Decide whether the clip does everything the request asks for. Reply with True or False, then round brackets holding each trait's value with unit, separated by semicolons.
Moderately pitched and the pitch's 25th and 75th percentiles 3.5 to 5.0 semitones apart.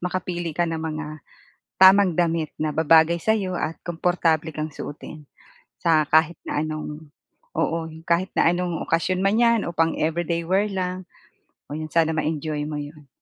False (165 Hz; 2.4 semitones)